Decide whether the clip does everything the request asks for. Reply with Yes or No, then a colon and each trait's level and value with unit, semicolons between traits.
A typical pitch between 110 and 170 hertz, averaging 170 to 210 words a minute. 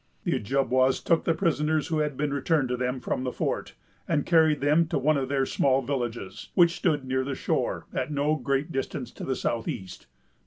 Yes: medium, 140 Hz; fast, 205 wpm